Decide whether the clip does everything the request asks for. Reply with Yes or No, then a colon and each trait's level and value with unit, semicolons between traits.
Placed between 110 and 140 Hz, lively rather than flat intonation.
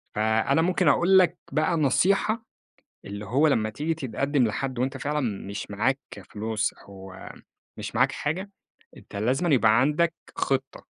Yes: low, 135 Hz; wide, 6.8 semitones